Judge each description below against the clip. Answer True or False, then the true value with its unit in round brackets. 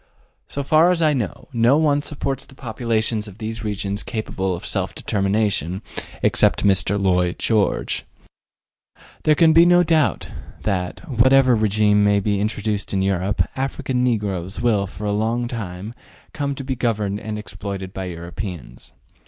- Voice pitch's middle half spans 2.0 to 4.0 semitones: False (4.7 semitones)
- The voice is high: False (110 Hz)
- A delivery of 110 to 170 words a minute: True (155 wpm)